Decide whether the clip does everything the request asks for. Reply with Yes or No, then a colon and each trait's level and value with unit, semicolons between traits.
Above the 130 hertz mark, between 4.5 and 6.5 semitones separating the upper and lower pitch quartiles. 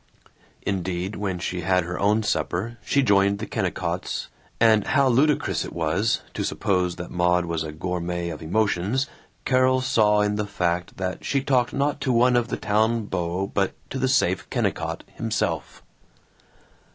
No: low, 100 Hz; average, 4.8 semitones